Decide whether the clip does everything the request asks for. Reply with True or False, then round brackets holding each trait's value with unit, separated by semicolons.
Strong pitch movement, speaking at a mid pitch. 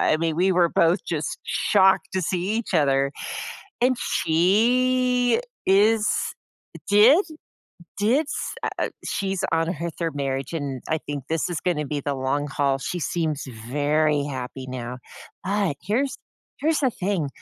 True (6.2 semitones; 165 Hz)